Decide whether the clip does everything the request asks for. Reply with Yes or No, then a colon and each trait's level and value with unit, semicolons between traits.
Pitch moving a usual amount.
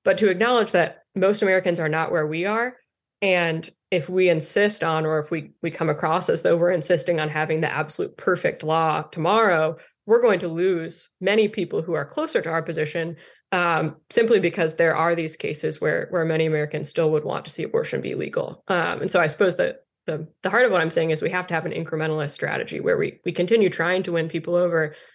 Yes: average, 3.1 semitones